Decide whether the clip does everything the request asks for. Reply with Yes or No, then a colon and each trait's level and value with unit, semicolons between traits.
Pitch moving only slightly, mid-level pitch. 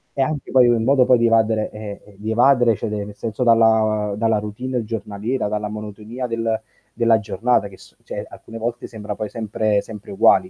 No: narrow, 2.0 semitones; low, 110 Hz